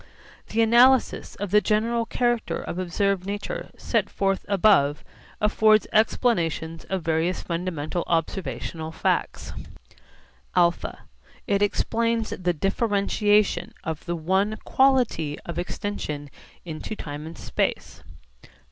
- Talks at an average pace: No, slow, 110 wpm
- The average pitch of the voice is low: No, high, 195 Hz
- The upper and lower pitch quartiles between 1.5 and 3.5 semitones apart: No, average, 4.7 semitones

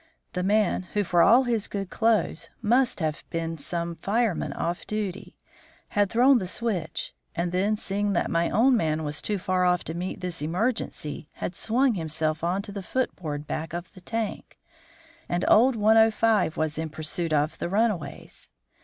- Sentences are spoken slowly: No, average, 175 wpm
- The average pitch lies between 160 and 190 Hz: Yes, medium, 185 Hz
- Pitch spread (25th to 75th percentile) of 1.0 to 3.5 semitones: No, average, 4.7 semitones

